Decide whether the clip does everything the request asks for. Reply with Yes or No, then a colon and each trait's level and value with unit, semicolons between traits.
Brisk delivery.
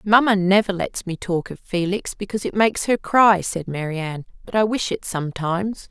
No: average, 195 wpm